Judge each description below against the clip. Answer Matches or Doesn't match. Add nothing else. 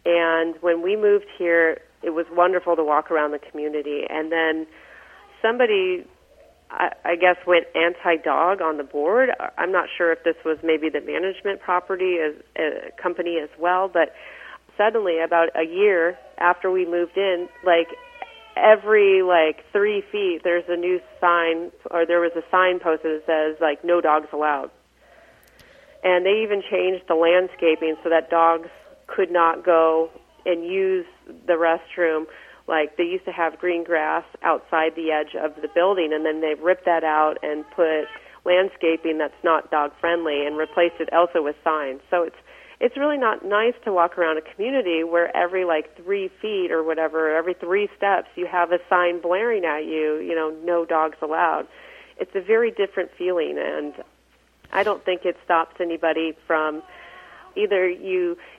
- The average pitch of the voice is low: Doesn't match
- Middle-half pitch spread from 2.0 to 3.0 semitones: Matches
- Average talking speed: Matches